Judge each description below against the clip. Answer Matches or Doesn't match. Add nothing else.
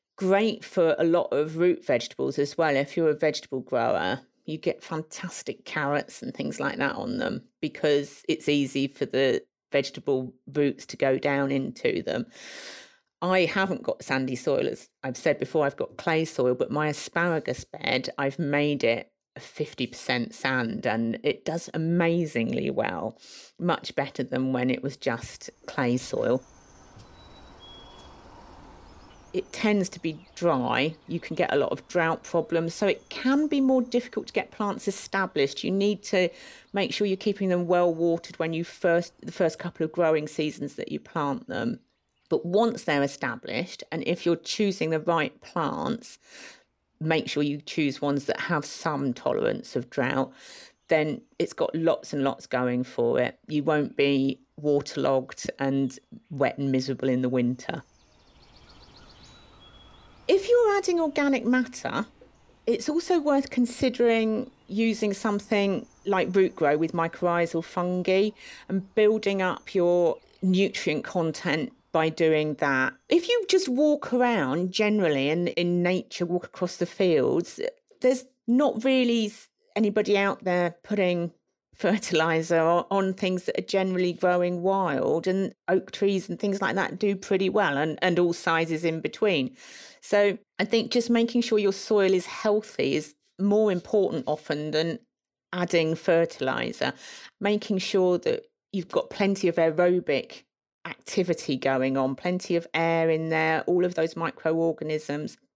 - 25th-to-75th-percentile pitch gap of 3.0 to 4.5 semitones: Doesn't match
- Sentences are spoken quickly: Doesn't match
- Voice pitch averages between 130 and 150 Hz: Doesn't match